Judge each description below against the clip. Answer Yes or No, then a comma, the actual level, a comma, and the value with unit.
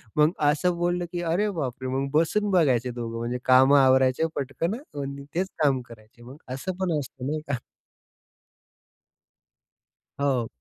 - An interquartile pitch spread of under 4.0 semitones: No, average, 4.8 semitones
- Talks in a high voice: No, medium, 140 Hz